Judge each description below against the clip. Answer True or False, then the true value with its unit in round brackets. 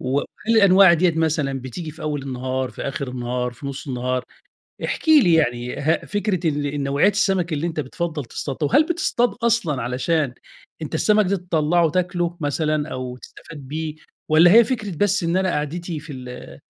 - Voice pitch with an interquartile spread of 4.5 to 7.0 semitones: True (4.8 semitones)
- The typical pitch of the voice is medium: True (155 Hz)